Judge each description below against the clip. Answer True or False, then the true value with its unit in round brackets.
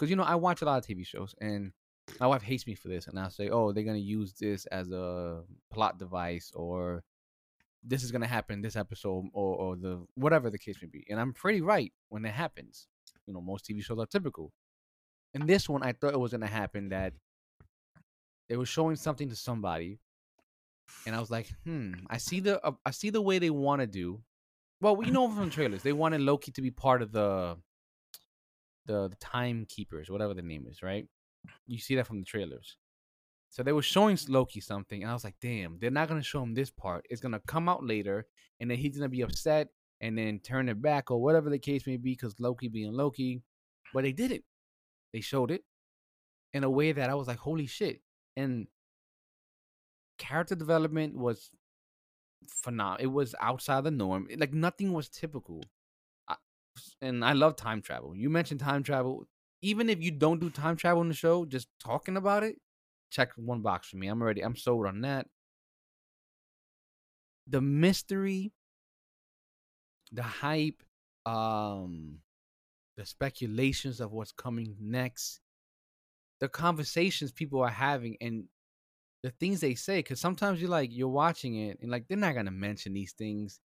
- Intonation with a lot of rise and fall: True (6.4 semitones)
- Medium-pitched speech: False (120 Hz)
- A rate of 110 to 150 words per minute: False (185 wpm)